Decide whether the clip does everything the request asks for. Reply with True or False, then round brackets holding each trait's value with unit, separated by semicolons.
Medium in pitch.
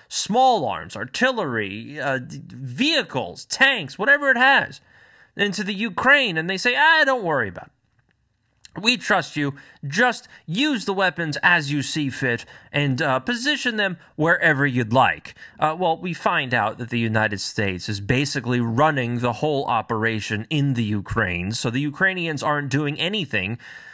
True (150 Hz)